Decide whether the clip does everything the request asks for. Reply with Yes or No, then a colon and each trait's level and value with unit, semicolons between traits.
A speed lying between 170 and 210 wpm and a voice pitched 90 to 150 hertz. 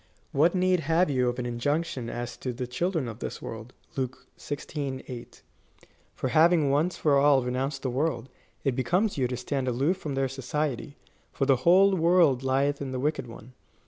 Yes: average, 185 wpm; low, 135 Hz